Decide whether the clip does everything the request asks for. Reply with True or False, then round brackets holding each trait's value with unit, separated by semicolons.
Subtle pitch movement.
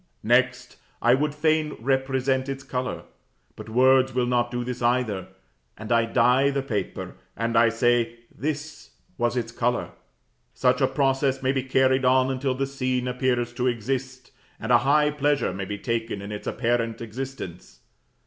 True (2.2 semitones)